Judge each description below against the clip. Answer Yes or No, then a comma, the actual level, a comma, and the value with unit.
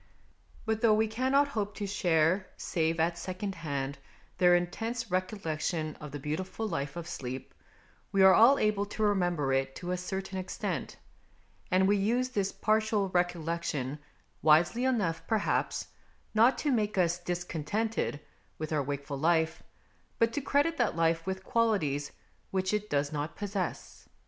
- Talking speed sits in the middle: Yes, average, 150 wpm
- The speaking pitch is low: No, medium, 185 Hz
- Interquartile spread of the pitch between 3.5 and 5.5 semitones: Yes, average, 5.0 semitones